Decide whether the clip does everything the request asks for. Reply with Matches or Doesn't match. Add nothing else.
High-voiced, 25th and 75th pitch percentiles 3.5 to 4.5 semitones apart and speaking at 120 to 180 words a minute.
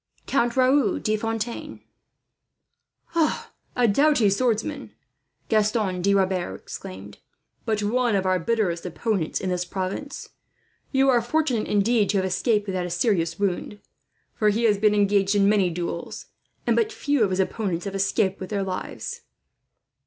Matches